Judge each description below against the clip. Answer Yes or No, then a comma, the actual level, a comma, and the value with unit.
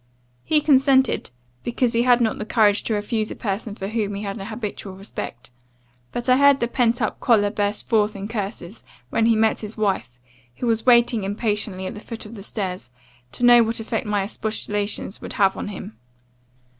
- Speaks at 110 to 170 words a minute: No, average, 195 wpm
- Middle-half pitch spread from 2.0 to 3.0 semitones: Yes, narrow, 2.6 semitones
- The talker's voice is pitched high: Yes, high, 215 Hz